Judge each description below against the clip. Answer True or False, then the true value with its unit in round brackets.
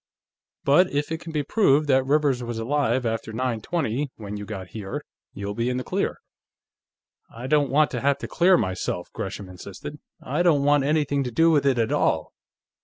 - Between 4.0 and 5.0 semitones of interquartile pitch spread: True (4.7 semitones)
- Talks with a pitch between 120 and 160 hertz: True (135 Hz)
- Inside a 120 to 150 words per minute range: False (195 wpm)